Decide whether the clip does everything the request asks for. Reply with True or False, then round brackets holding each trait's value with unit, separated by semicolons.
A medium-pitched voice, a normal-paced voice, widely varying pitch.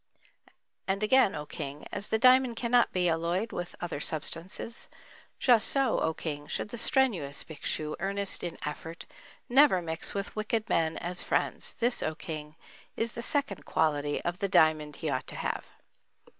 True (180 Hz; 165 wpm; 6.4 semitones)